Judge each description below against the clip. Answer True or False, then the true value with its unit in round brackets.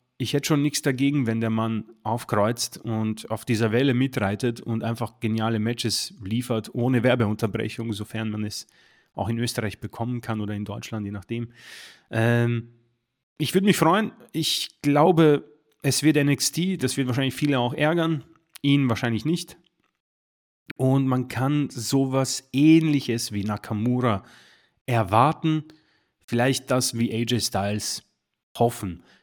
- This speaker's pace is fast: False (140 wpm)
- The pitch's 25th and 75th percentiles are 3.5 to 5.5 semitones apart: True (3.9 semitones)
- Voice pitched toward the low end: True (120 Hz)